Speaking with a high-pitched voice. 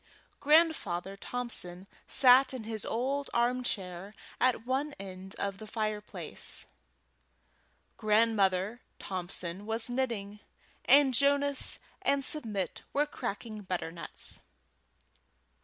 Yes: high, 225 Hz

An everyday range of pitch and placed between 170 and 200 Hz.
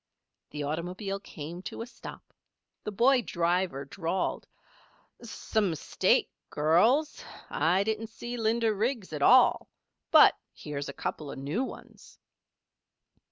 No: wide, 6.2 semitones; high, 190 Hz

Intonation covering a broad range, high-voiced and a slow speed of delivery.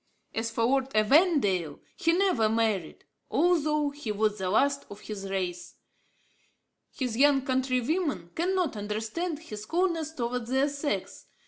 Yes: wide, 6.2 semitones; very high, 255 Hz; slow, 130 wpm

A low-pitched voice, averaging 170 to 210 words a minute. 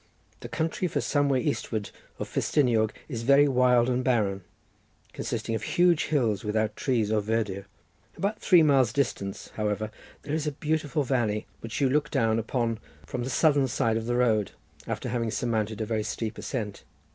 Yes: low, 120 Hz; average, 175 wpm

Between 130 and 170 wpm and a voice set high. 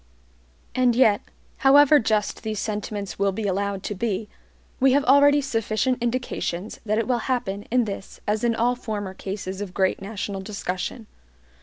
Yes: average, 160 wpm; high, 215 Hz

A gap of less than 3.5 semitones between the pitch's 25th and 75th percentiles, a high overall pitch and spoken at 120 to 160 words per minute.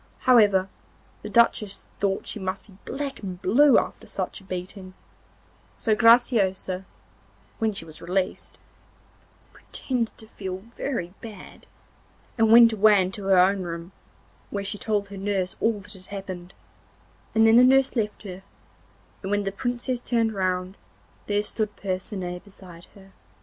Yes: average, 3.0 semitones; high, 200 Hz; average, 150 wpm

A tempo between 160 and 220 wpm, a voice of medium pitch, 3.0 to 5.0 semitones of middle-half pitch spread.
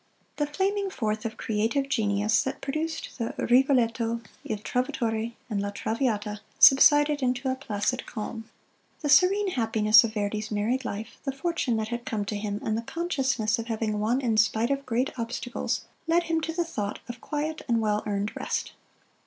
No: average, 175 wpm; high, 235 Hz; average, 4.2 semitones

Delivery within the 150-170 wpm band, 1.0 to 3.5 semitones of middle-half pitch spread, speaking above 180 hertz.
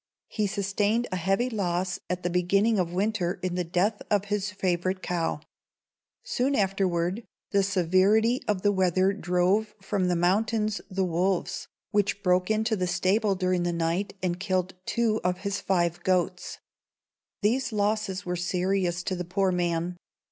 Yes: average, 155 wpm; narrow, 2.4 semitones; high, 190 Hz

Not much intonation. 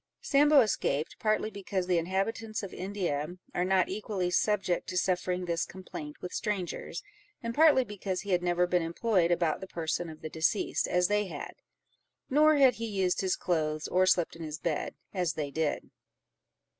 No: average, 3.6 semitones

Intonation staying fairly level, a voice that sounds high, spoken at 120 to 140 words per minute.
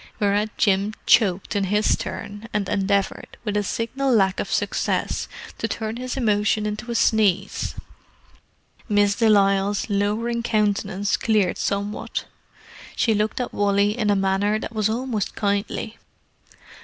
Yes: narrow, 1.6 semitones; high, 210 Hz; slow, 135 wpm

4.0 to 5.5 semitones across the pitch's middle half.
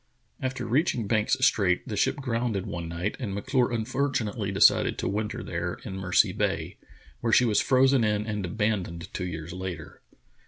Yes: average, 4.5 semitones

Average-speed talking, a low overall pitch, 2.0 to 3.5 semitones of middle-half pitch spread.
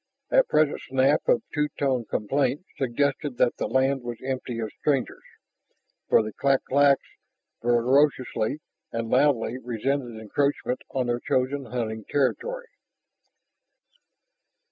No: slow, 120 wpm; low, 130 Hz; average, 3.0 semitones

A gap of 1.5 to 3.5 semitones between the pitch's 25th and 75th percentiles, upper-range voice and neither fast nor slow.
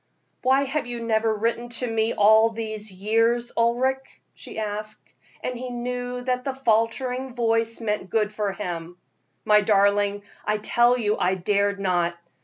Yes: average, 2.7 semitones; high, 225 Hz; average, 155 wpm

